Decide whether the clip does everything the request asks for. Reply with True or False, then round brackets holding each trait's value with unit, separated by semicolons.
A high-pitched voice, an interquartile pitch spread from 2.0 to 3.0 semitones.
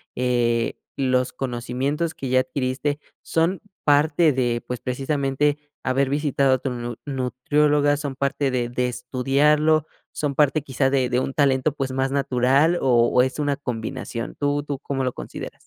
False (135 Hz; 2.4 semitones)